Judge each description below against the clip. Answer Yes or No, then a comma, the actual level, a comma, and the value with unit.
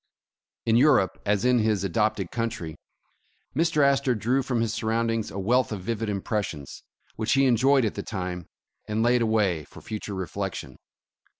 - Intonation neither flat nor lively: Yes, average, 3.7 semitones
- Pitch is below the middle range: Yes, low, 110 Hz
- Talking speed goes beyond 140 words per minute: Yes, average, 165 wpm